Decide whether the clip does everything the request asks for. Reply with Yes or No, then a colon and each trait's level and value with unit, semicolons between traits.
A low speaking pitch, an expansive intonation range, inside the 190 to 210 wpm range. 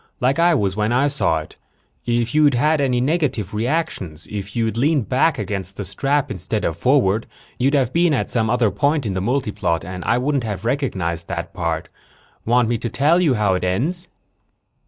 Yes: low, 120 Hz; wide, 6.3 semitones; average, 195 wpm